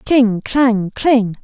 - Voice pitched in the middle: No, high, 230 Hz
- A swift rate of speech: No, slow, 125 wpm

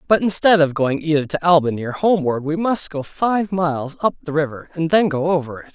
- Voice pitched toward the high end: No, medium, 160 Hz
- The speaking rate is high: Yes, fast, 230 wpm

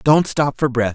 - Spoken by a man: Yes, male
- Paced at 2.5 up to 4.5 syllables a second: Yes, 4.4 syllables/s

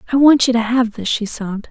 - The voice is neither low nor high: No, high, 235 Hz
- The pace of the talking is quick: Yes, fast, 280 wpm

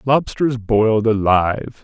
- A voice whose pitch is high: No, low, 115 Hz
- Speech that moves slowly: Yes, slow, 100 wpm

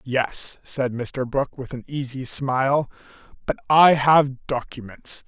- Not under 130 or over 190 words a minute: Yes, slow, 135 wpm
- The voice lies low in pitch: Yes, low, 130 Hz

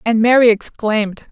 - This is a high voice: Yes, high, 225 Hz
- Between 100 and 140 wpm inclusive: Yes, slow, 135 wpm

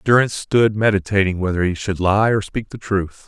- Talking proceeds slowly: No, average, 200 wpm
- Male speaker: Yes, male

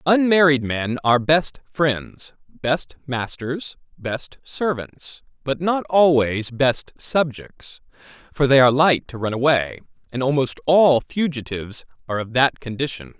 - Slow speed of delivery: Yes, slow, 130 wpm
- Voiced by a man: Yes, male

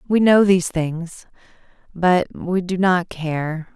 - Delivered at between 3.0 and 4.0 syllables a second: Yes, 3.5 syllables/s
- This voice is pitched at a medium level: Yes, medium, 175 Hz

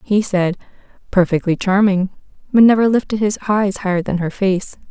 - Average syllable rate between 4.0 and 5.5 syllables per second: Yes, 5.1 syllables/s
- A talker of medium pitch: No, high, 195 Hz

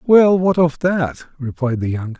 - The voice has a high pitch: No, medium, 150 Hz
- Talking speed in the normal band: Yes, average, 190 wpm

